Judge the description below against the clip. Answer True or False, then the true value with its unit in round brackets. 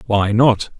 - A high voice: False (110 Hz)